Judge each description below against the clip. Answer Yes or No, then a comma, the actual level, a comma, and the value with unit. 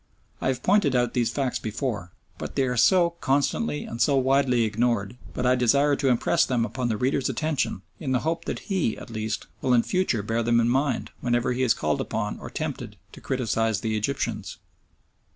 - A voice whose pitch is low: Yes, low, 125 Hz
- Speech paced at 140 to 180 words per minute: No, average, 200 wpm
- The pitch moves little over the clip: No, average, 3.3 semitones